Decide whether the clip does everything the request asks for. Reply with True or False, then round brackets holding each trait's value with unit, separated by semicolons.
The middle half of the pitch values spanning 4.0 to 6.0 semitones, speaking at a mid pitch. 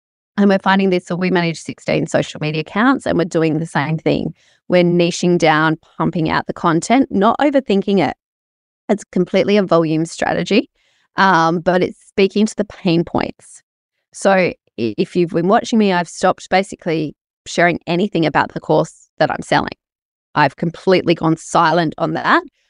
False (3.4 semitones; 180 Hz)